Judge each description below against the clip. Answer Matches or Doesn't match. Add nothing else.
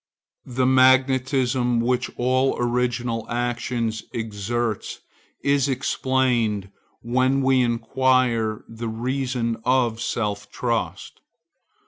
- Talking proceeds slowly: Matches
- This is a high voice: Doesn't match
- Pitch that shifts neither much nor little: Doesn't match